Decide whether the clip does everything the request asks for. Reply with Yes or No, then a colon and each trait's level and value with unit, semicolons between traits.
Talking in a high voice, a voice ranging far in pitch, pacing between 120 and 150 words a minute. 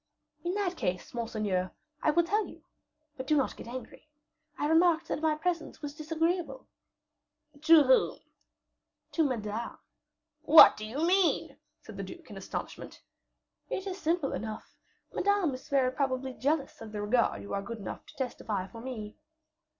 No: very high, 275 Hz; wide, 6.2 semitones; average, 160 wpm